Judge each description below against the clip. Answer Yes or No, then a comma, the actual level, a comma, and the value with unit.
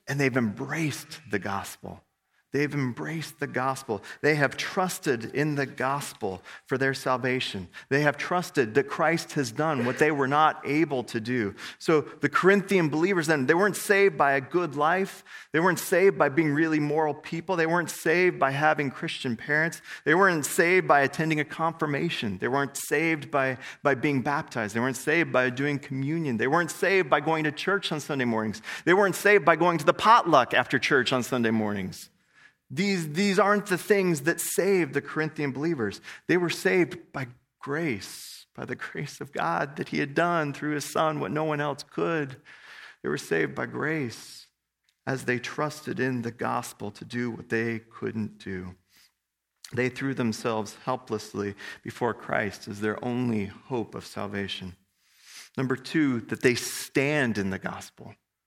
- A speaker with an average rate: Yes, average, 175 wpm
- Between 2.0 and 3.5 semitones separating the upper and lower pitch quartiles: No, average, 4.6 semitones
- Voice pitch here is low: No, medium, 145 Hz